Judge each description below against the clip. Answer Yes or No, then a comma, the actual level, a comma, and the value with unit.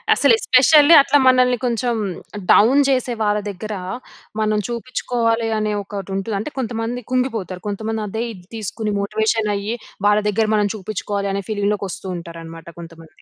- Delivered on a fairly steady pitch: No, average, 3.1 semitones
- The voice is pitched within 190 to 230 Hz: Yes, high, 215 Hz